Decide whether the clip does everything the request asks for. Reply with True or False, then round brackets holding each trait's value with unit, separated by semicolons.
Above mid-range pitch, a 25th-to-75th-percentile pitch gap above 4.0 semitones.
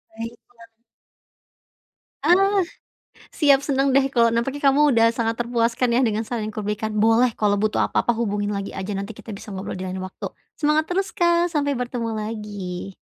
True (230 Hz; 4.5 semitones)